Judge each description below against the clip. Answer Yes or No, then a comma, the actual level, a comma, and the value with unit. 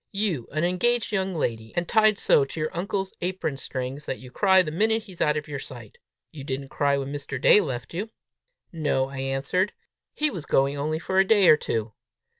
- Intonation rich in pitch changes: Yes, wide, 5.8 semitones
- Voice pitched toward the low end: No, medium, 155 Hz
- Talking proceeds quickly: Yes, fast, 210 wpm